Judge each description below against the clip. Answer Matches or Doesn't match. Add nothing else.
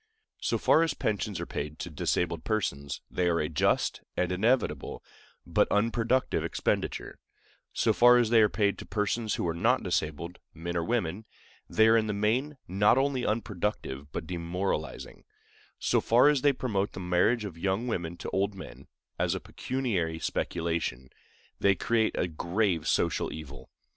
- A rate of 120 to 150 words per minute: Doesn't match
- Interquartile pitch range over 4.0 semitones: Matches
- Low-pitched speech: Matches